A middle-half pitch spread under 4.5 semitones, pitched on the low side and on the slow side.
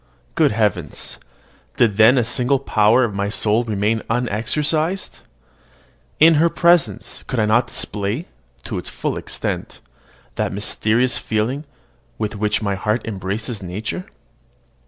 Yes: average, 3.5 semitones; low, 110 Hz; slow, 130 wpm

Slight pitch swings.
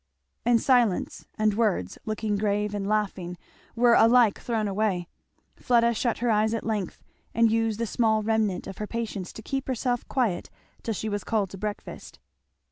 Yes: narrow, 2.1 semitones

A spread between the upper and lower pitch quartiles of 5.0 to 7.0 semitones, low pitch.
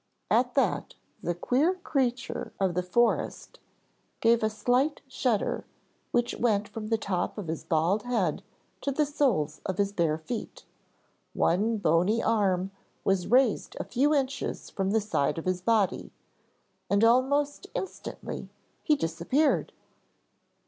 No: wide, 5.6 semitones; high, 215 Hz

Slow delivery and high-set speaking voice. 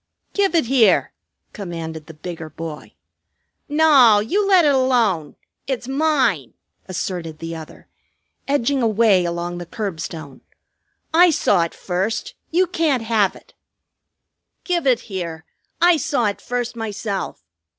Yes: slow, 130 wpm; high, 220 Hz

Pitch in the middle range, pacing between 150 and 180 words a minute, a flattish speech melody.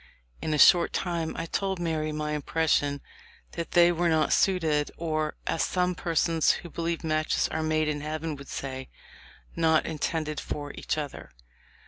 Yes: medium, 160 Hz; average, 160 wpm; narrow, 1.7 semitones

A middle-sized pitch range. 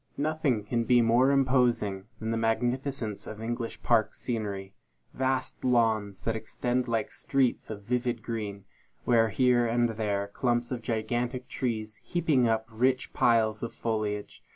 No: narrow, 2.3 semitones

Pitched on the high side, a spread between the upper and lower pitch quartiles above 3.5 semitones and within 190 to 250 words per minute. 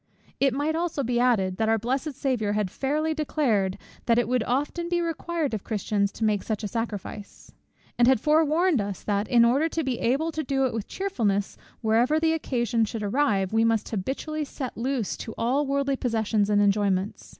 Yes: high, 240 Hz; average, 5.3 semitones; average, 195 wpm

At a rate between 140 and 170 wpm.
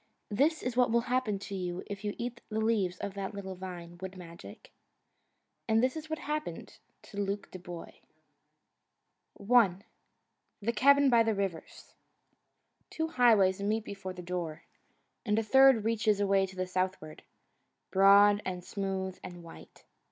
Yes: average, 150 wpm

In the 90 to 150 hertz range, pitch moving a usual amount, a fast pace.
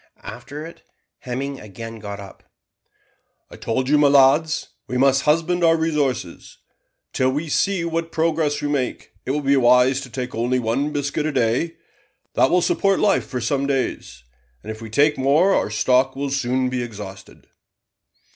No: low, 135 Hz; average, 3.5 semitones; average, 170 wpm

